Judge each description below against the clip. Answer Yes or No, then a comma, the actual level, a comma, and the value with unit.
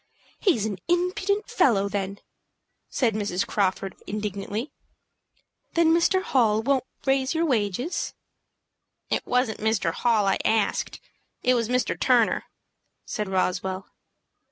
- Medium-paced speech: No, slow, 115 wpm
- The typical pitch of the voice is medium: No, high, 220 Hz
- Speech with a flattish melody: No, wide, 5.4 semitones